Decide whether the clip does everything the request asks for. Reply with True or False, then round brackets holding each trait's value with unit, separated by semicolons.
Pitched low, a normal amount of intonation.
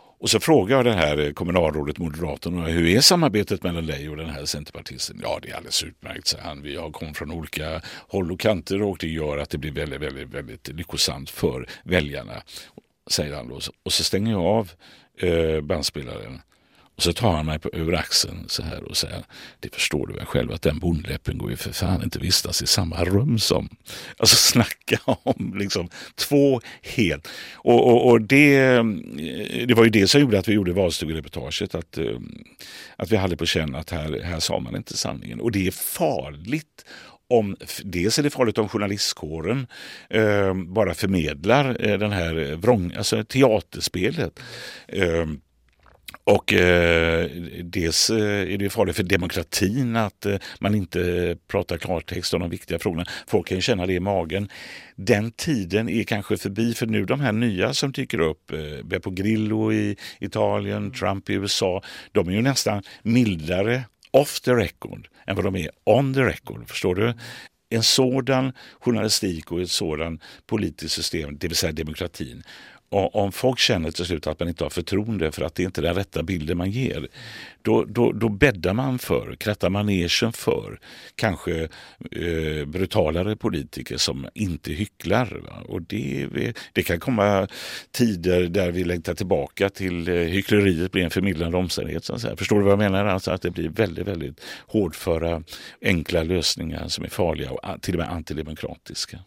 True (95 Hz; 4.5 semitones)